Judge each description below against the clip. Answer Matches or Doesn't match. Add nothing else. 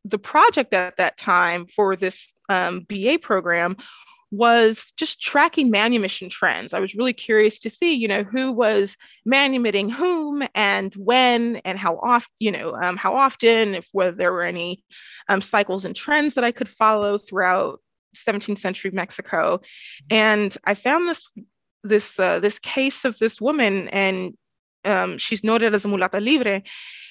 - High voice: Matches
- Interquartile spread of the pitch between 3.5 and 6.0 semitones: Matches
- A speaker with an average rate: Matches